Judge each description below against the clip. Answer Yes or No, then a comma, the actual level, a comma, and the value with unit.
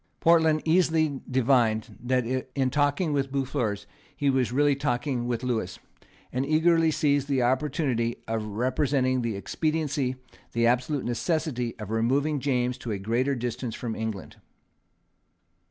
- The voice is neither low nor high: No, low, 130 Hz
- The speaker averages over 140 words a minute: No, slow, 135 wpm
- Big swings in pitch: No, average, 3.5 semitones